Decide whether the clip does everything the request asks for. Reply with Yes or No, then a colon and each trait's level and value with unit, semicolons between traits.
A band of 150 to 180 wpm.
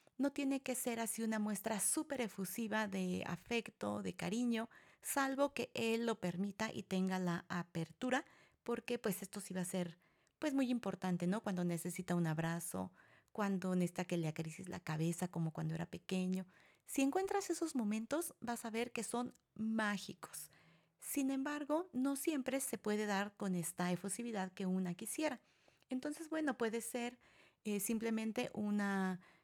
Yes: average, 160 wpm